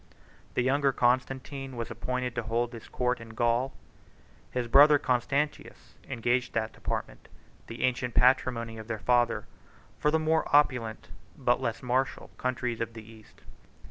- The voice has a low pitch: Yes, low, 125 Hz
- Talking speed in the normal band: Yes, average, 150 wpm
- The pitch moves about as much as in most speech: No, narrow, 2.2 semitones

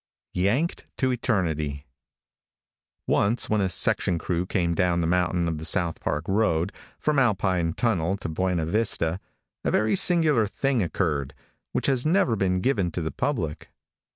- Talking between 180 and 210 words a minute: No, average, 155 wpm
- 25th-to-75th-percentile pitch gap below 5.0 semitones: No, wide, 5.5 semitones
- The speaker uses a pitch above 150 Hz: No, very low, 95 Hz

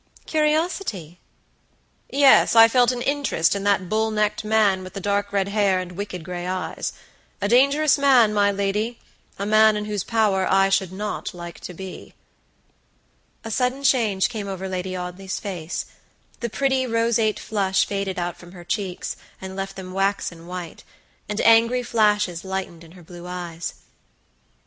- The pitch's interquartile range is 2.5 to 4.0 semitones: Yes, average, 3.5 semitones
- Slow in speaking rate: No, average, 160 wpm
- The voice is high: Yes, high, 200 Hz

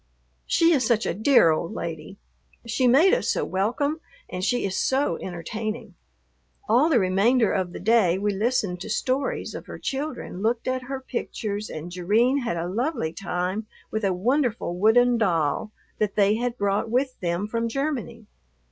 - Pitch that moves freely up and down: No, average, 4.9 semitones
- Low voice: No, high, 220 Hz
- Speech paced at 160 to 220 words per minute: Yes, average, 170 wpm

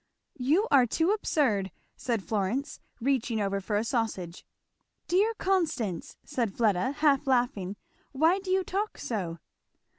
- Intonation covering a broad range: Yes, wide, 7.5 semitones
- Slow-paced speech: Yes, slow, 130 wpm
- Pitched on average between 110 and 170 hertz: No, very high, 250 Hz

